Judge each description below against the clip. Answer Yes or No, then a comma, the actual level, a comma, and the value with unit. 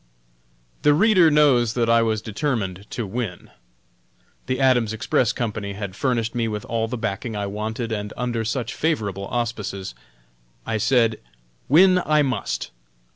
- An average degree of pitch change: Yes, average, 3.4 semitones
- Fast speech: No, average, 145 wpm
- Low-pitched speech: Yes, low, 115 Hz